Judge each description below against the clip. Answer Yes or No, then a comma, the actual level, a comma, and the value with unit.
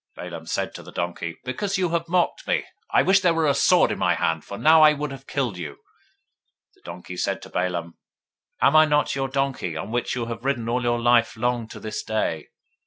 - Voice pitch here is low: Yes, low, 120 Hz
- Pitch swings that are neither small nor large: No, wide, 8.3 semitones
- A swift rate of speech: Yes, fast, 230 wpm